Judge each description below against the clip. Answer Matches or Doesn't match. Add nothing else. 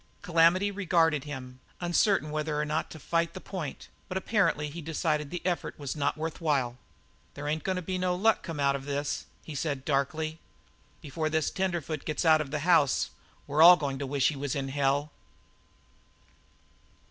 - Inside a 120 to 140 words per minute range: Doesn't match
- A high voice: Doesn't match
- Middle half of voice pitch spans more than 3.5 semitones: Doesn't match